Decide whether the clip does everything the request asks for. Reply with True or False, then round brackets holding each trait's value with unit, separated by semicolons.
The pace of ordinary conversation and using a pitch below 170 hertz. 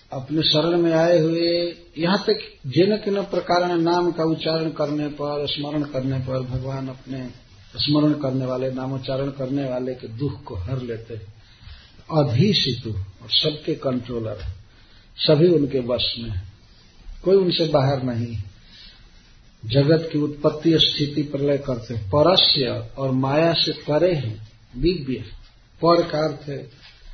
True (130 wpm; 140 Hz)